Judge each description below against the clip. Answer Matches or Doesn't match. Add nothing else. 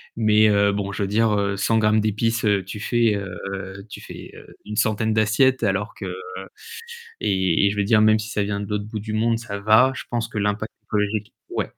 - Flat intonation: Matches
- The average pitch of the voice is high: Doesn't match